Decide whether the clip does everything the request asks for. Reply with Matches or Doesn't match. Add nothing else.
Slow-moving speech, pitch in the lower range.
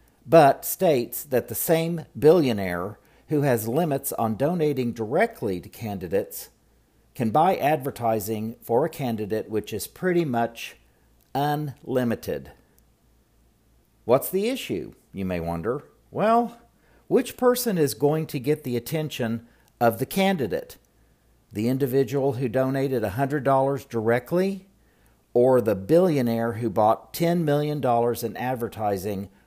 Matches